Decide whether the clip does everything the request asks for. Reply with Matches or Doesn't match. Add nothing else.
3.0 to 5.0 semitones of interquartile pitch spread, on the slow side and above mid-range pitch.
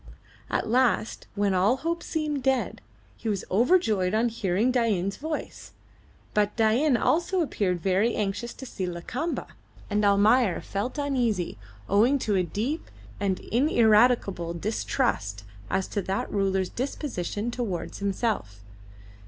Matches